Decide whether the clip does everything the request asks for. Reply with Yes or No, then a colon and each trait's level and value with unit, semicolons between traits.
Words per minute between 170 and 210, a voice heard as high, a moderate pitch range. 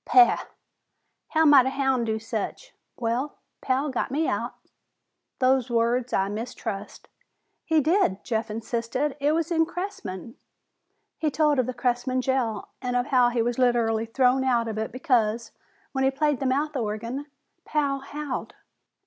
No: average, 155 wpm; very high, 255 Hz; average, 3.7 semitones